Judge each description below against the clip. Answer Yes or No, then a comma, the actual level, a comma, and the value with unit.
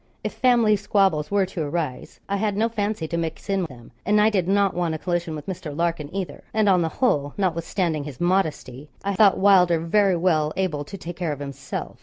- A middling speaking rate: No, fast, 215 wpm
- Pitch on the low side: No, medium, 175 Hz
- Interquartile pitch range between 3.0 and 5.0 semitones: Yes, average, 4.1 semitones